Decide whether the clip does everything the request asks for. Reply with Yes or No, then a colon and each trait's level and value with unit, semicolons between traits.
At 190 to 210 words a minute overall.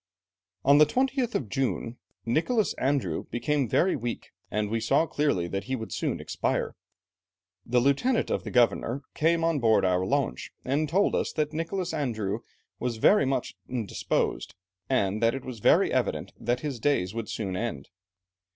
No: average, 165 wpm